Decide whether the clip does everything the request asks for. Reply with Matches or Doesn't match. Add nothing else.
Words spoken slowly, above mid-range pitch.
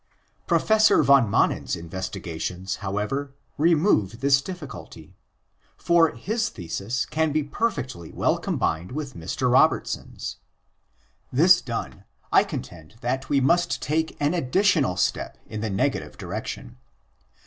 Doesn't match